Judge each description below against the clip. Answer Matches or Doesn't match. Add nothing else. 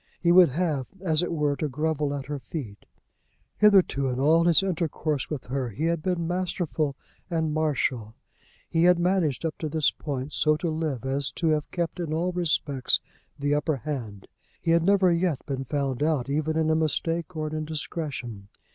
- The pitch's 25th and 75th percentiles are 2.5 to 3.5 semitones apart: Matches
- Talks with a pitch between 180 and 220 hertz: Doesn't match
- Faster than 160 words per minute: Matches